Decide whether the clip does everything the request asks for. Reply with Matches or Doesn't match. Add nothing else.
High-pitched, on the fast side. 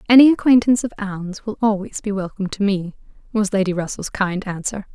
Doesn't match